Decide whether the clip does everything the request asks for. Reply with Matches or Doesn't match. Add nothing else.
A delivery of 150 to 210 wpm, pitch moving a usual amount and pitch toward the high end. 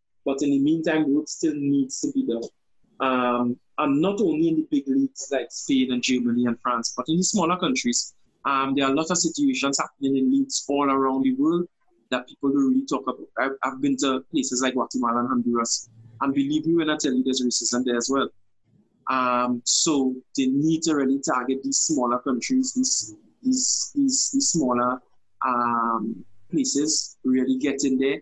Doesn't match